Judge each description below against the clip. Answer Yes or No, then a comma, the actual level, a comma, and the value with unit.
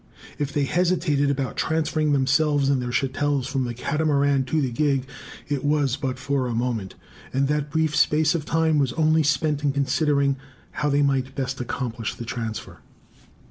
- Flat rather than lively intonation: Yes, narrow, 2.3 semitones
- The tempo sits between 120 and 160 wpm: No, average, 175 wpm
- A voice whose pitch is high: No, medium, 140 Hz